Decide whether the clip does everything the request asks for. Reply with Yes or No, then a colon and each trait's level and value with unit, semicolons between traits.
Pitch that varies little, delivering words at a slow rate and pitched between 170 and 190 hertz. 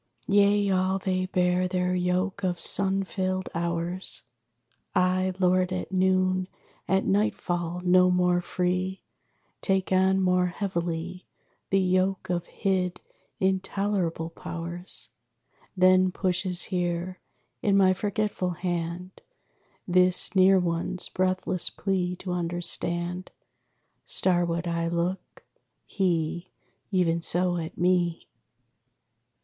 Yes: narrow, 1.2 semitones; slow, 105 wpm; medium, 185 Hz